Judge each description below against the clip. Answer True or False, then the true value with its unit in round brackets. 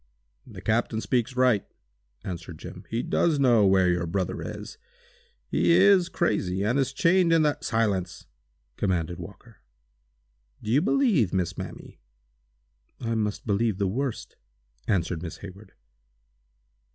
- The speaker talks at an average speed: False (130 wpm)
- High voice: False (110 Hz)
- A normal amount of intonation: False (6.4 semitones)